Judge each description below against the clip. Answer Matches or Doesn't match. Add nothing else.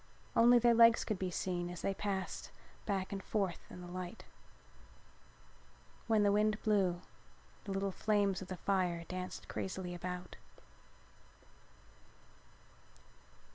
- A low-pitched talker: Doesn't match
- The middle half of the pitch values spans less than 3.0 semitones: Matches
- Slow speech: Matches